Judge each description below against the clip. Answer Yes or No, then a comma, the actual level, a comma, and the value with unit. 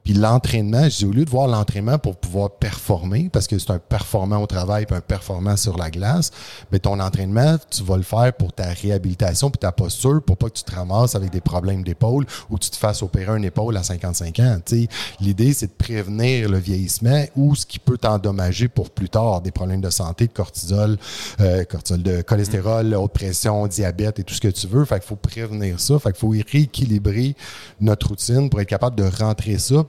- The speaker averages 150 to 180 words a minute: No, fast, 220 wpm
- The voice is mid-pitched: No, low, 105 Hz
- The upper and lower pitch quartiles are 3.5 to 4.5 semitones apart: Yes, average, 3.9 semitones